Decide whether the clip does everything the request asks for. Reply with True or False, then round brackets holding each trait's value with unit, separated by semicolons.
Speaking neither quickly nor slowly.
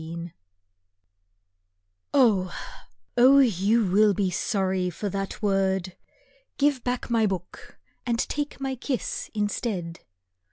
False (110 wpm)